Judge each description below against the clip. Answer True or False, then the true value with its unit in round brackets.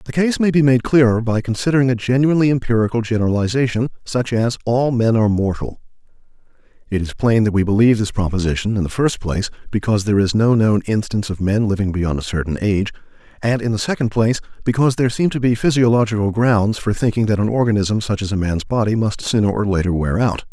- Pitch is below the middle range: True (110 Hz)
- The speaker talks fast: True (210 wpm)